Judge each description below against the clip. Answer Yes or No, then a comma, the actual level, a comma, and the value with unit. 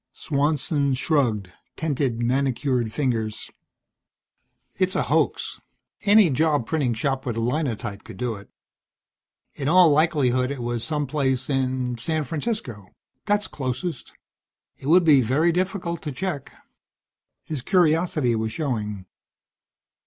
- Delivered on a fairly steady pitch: No, average, 4.7 semitones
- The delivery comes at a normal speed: No, slow, 125 wpm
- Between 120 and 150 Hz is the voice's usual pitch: Yes, low, 135 Hz